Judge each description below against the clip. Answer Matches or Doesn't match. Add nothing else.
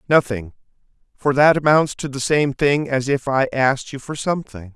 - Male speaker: Matches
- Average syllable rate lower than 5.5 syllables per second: Matches